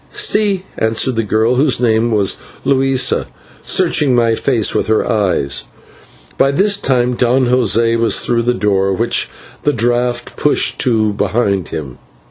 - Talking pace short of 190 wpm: Yes, average, 145 wpm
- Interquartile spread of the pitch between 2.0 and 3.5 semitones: Yes, average, 2.9 semitones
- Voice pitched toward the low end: Yes, low, 120 Hz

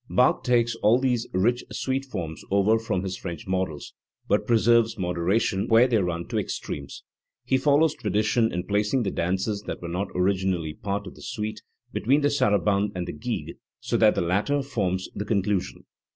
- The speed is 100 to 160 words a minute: No, average, 185 wpm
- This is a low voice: Yes, low, 105 Hz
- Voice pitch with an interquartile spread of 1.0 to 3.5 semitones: No, average, 4.2 semitones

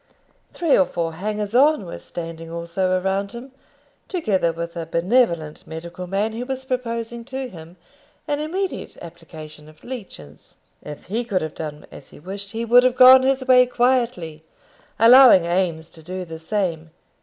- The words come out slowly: No, average, 165 wpm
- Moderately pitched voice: No, high, 195 Hz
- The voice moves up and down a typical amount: No, wide, 6.9 semitones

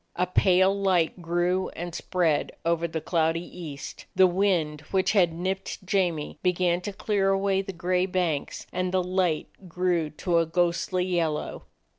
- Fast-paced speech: No, average, 160 wpm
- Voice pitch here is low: No, medium, 180 Hz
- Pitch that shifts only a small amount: Yes, narrow, 2.0 semitones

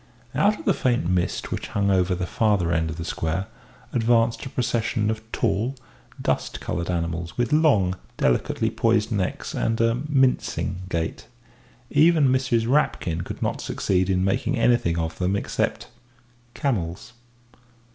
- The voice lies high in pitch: No, low, 105 Hz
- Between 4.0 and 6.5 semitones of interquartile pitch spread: Yes, wide, 5.5 semitones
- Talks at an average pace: Yes, average, 145 wpm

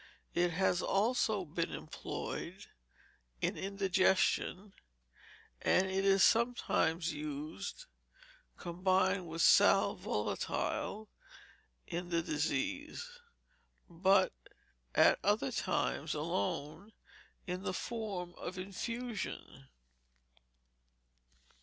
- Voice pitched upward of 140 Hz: Yes, medium, 185 Hz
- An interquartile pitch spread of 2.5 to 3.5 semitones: Yes, average, 3.2 semitones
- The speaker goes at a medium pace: No, slow, 80 wpm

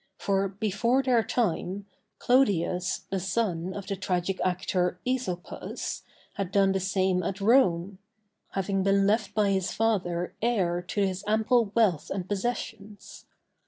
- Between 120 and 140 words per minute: Yes, slow, 135 wpm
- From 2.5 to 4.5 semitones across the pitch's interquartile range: Yes, average, 2.8 semitones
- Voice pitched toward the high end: Yes, high, 195 Hz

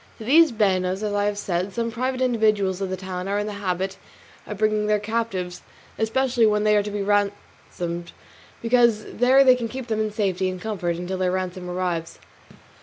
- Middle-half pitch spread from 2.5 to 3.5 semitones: Yes, average, 3.2 semitones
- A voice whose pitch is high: Yes, high, 205 Hz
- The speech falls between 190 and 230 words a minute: Yes, average, 195 wpm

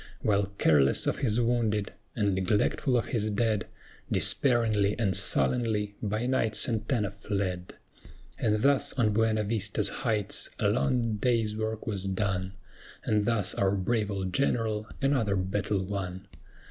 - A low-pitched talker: Yes, low, 105 Hz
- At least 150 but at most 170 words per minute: No, slow, 135 wpm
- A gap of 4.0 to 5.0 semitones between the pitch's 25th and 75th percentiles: No, narrow, 2.6 semitones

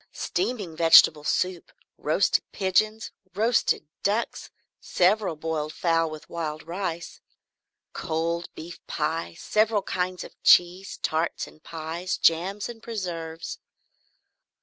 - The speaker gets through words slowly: Yes, slow, 110 wpm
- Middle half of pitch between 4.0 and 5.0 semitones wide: No, average, 3.5 semitones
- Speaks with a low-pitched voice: No, medium, 170 Hz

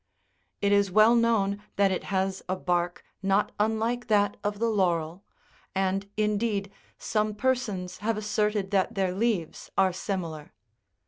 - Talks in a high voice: Yes, high, 200 Hz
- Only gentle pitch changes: Yes, narrow, 2.2 semitones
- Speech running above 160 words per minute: No, average, 140 wpm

